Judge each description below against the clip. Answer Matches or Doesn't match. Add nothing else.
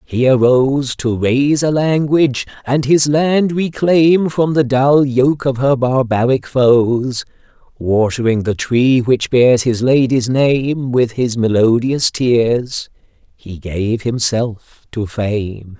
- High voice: Doesn't match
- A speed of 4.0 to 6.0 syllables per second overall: Doesn't match